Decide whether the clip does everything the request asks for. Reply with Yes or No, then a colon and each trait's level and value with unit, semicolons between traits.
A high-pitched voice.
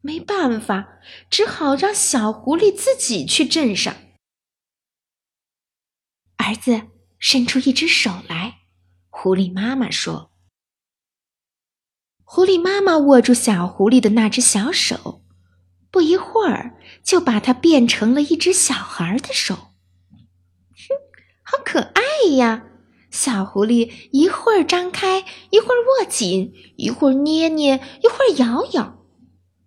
Yes: very high, 250 Hz